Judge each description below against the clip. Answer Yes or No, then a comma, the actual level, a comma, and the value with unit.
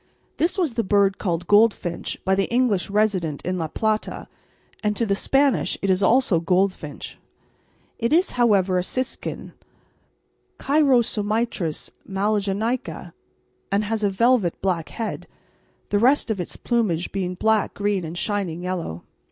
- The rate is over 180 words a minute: No, average, 140 wpm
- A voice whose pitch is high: Yes, high, 205 Hz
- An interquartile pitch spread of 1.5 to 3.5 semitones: No, average, 3.9 semitones